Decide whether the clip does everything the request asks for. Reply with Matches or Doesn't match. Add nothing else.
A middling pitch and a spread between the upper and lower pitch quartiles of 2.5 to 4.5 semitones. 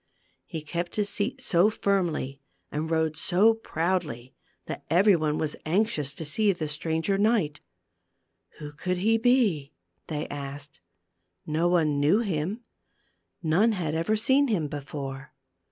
Doesn't match